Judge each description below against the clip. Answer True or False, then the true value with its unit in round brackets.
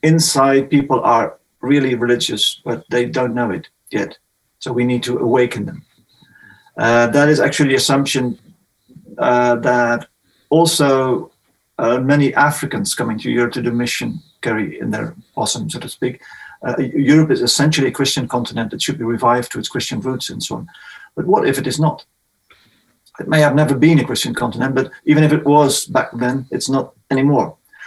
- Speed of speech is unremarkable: True (180 wpm)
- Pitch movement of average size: True (3.0 semitones)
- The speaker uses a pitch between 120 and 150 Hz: True (135 Hz)